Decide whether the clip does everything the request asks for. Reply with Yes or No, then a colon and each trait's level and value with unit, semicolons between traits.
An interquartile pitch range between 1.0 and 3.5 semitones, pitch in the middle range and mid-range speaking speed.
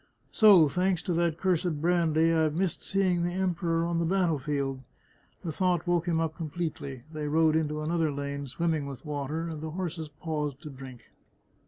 Yes: average, 2.7 semitones; medium, 160 Hz; average, 185 wpm